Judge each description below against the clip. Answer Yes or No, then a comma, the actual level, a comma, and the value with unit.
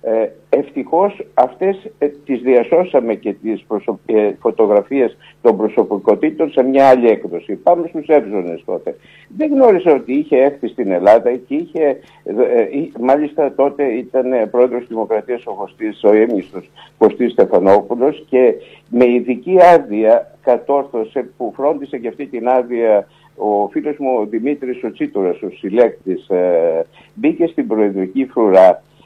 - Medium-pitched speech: Yes, medium, 145 Hz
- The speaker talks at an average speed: Yes, average, 130 wpm